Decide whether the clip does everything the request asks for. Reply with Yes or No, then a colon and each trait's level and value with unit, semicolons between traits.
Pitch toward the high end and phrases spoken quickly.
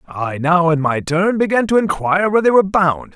No: medium, 175 Hz; fast, 230 wpm